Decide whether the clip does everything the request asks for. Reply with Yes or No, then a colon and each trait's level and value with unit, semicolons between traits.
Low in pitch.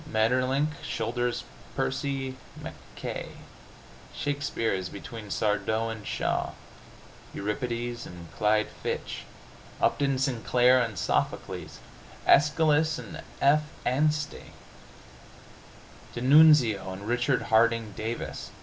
Yes: low, 120 Hz